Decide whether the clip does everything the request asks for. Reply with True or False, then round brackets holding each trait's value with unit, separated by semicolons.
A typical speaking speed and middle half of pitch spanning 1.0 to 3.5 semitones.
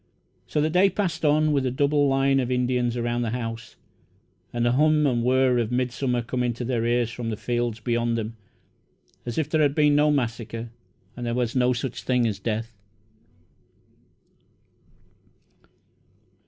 True (165 wpm; 2.7 semitones)